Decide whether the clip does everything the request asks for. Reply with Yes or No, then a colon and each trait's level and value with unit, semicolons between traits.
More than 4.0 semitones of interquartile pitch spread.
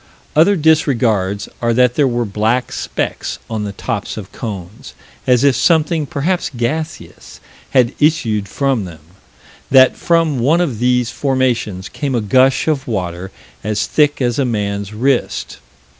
Yes: average, 5.0 semitones